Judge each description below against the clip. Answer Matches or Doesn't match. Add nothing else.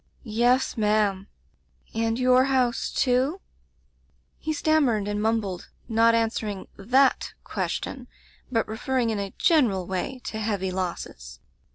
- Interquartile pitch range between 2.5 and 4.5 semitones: Matches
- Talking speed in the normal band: Doesn't match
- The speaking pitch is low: Doesn't match